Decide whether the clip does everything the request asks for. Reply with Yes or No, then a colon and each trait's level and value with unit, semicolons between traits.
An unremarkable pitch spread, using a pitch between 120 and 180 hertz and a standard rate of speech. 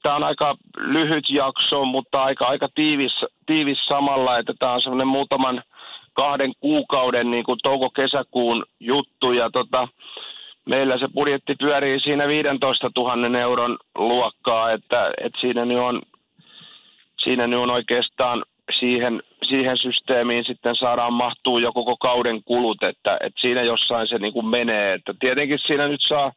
No: narrow, 2.2 semitones; low, 125 Hz; average, 145 wpm